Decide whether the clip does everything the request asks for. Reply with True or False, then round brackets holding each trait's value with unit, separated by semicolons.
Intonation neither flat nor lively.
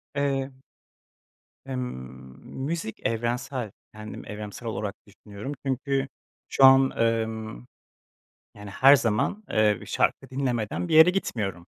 True (4.1 semitones)